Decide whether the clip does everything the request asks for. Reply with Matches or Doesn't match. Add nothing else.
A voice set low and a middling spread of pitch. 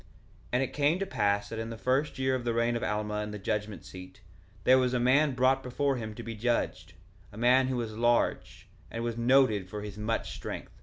Matches